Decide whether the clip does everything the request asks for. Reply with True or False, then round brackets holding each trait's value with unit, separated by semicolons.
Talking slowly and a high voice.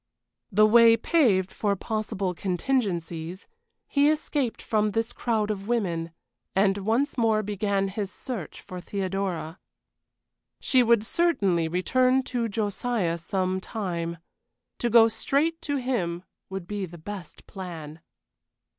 True (125 wpm; 205 Hz)